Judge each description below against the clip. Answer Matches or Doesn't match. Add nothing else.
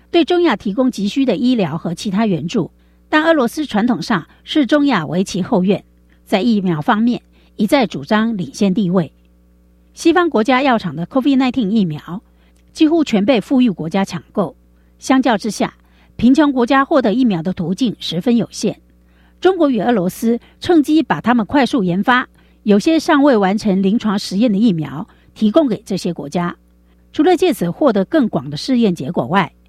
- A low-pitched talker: Doesn't match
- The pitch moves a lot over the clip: Matches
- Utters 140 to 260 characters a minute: Doesn't match